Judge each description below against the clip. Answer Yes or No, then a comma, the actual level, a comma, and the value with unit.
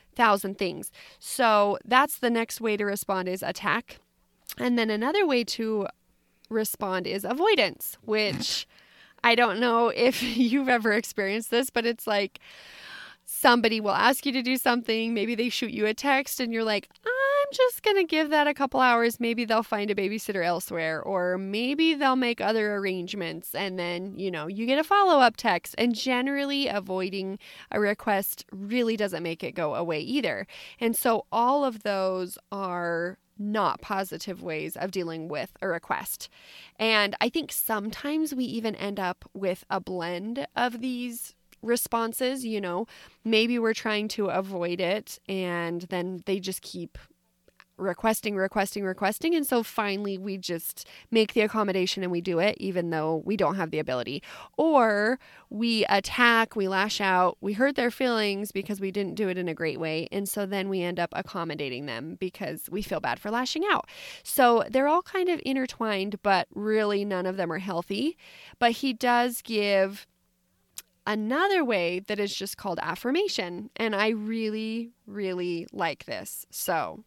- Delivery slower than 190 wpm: Yes, average, 170 wpm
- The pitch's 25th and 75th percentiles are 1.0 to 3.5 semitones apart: No, average, 4.2 semitones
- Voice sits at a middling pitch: No, high, 210 Hz